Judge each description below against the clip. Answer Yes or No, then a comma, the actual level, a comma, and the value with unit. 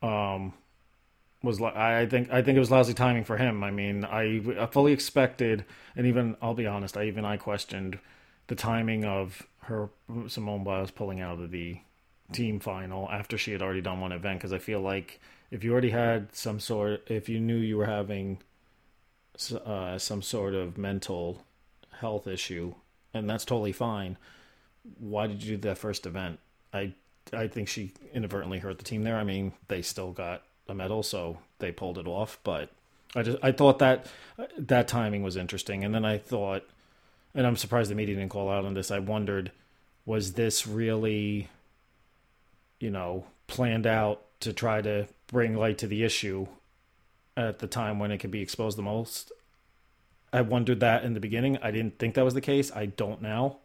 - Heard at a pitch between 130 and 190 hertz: No, low, 105 Hz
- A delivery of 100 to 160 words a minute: No, average, 185 wpm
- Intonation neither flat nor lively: Yes, average, 3.1 semitones